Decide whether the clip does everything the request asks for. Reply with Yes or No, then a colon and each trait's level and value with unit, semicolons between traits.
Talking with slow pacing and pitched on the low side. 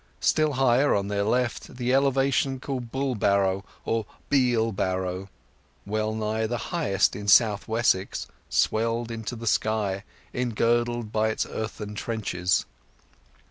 Yes: slow, 120 wpm; low, 110 Hz